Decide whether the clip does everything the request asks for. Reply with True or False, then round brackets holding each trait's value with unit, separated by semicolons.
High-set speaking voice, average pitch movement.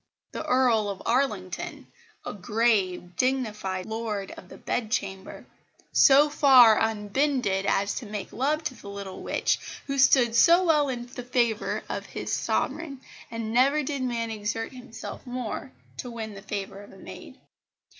True (230 Hz; 4.1 semitones)